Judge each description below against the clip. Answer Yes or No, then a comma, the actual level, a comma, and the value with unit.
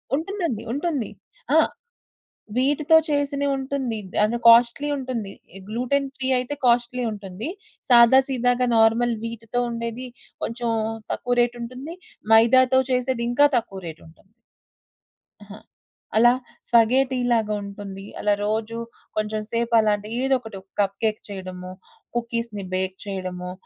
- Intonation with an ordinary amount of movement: Yes, average, 3.3 semitones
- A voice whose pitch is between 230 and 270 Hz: Yes, high, 235 Hz